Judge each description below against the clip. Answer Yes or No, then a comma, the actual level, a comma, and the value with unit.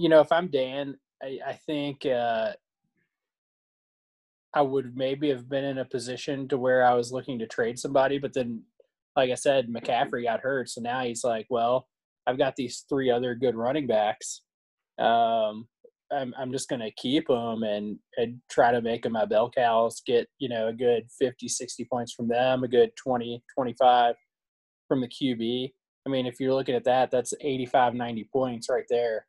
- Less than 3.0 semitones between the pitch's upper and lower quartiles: Yes, narrow, 2.5 semitones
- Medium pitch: No, low, 125 Hz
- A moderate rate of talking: Yes, average, 190 wpm